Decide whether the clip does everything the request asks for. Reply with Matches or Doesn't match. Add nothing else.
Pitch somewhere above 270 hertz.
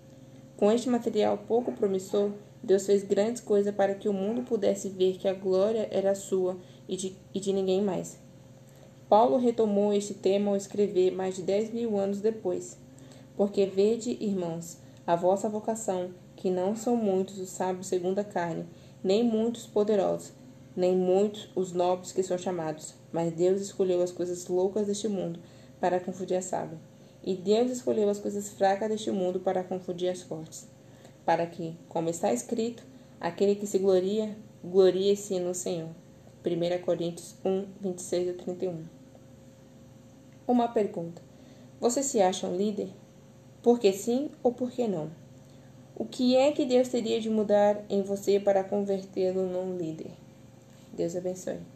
Doesn't match